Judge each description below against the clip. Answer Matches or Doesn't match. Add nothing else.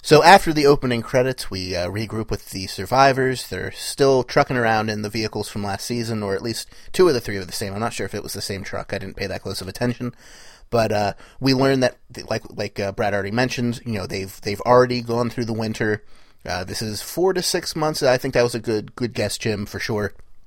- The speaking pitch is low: Matches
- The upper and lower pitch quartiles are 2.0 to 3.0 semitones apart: Doesn't match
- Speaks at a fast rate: Matches